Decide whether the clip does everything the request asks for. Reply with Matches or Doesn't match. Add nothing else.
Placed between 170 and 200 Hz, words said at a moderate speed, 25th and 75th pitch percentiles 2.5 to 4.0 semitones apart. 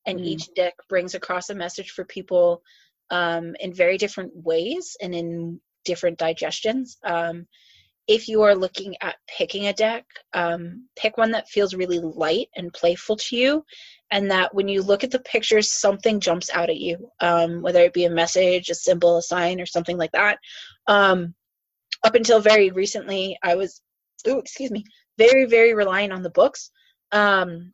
Matches